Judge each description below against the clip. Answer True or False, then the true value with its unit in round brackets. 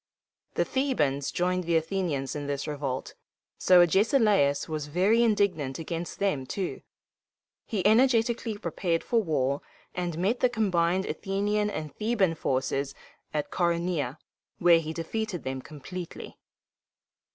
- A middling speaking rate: False (125 wpm)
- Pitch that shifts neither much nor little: False (5.7 semitones)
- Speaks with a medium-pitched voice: True (175 Hz)